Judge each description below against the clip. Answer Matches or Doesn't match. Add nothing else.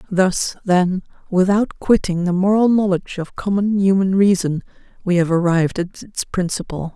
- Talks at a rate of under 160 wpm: Matches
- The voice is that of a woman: Matches